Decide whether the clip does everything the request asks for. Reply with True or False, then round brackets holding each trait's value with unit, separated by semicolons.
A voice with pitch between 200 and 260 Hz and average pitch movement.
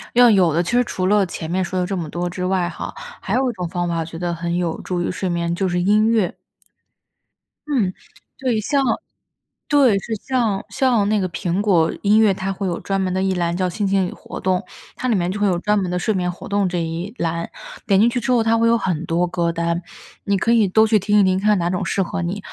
False (190 Hz; 3.4 semitones)